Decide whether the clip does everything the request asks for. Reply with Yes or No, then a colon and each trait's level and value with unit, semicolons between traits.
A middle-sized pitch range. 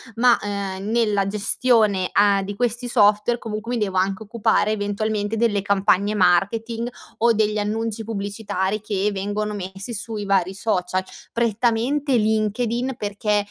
No: narrow, 2.3 semitones